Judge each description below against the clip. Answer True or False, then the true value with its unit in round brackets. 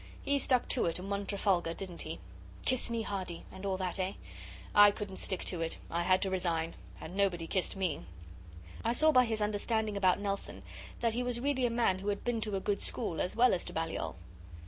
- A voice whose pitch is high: True (200 Hz)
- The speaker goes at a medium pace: False (220 wpm)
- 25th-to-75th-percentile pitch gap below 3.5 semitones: False (3.8 semitones)